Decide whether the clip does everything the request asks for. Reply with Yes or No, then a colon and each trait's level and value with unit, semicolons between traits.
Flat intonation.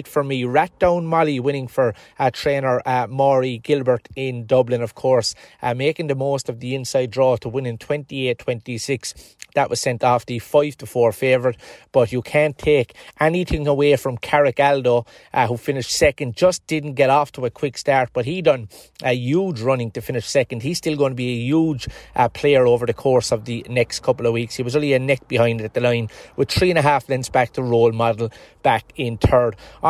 No: average, 3.1 semitones